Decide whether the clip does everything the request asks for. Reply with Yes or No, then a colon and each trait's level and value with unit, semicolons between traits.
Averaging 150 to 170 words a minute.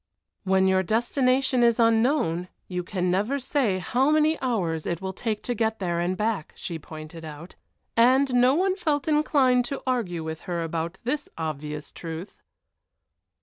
Yes: average, 160 wpm